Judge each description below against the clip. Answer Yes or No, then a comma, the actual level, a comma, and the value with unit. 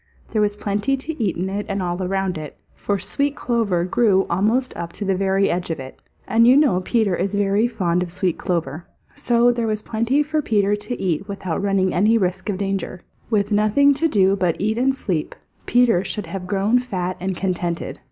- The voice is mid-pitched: No, high, 200 Hz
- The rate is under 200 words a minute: No, fast, 205 wpm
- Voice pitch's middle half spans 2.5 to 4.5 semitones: Yes, average, 3.8 semitones